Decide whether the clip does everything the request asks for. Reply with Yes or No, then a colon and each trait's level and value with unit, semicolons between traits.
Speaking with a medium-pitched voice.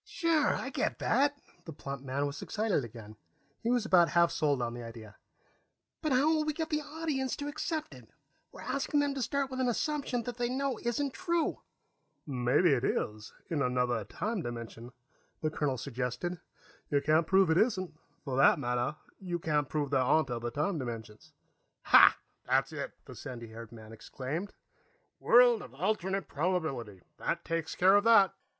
Yes: medium, 165 Hz